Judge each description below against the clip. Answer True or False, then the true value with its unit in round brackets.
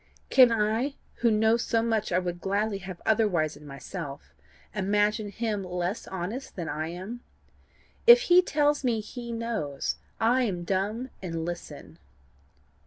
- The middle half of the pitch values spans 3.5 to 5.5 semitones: True (4.6 semitones)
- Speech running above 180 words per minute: False (145 wpm)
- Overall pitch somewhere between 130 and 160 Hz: False (210 Hz)